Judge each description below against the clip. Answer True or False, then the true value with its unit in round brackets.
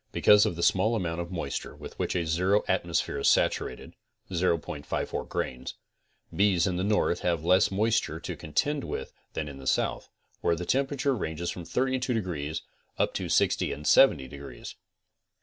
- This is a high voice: False (90 Hz)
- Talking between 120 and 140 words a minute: False (170 wpm)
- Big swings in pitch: False (4.6 semitones)